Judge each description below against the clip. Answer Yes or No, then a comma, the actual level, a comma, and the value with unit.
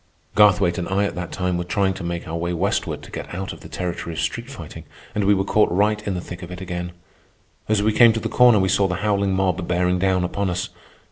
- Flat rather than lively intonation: Yes, narrow, 2.3 semitones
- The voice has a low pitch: Yes, very low, 95 Hz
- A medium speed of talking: No, fast, 260 wpm